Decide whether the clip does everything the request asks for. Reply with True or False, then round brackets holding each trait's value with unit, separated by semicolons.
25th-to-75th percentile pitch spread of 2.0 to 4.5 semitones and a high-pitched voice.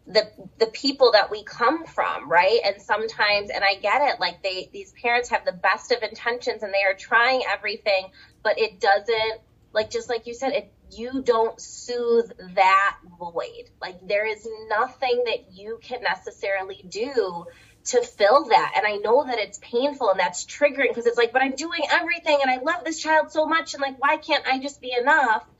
False (5.4 semitones; 235 Hz)